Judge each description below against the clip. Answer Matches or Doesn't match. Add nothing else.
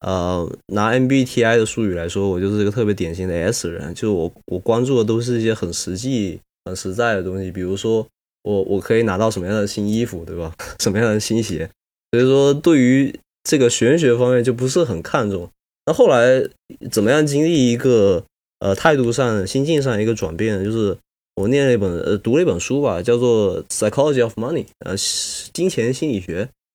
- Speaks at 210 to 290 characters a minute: Doesn't match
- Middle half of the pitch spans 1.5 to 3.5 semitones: Doesn't match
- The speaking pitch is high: Doesn't match